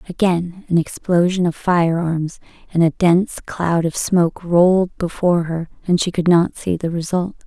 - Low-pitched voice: No, medium, 175 Hz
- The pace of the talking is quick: No, average, 170 wpm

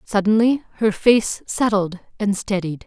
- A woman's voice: Yes, female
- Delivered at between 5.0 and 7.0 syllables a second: No, 4.2 syllables/s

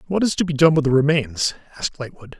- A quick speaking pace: Yes, fast, 250 wpm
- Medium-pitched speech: Yes, medium, 145 Hz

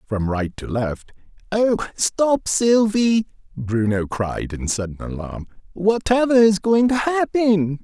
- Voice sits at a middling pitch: Yes, medium, 175 Hz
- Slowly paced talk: Yes, slow, 125 wpm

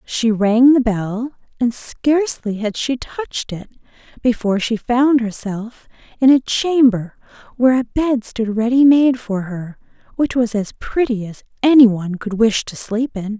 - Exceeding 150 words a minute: Yes, average, 160 wpm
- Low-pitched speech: No, high, 235 Hz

